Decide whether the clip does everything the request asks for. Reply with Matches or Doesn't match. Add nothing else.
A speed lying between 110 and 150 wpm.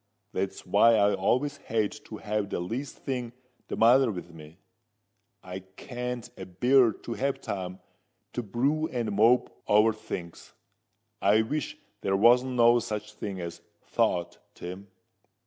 Matches